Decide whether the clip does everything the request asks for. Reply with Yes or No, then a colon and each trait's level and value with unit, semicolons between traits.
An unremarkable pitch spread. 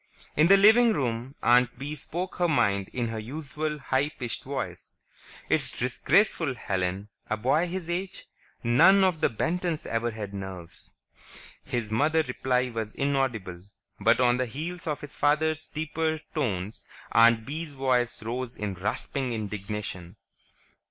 No: wide, 5.8 semitones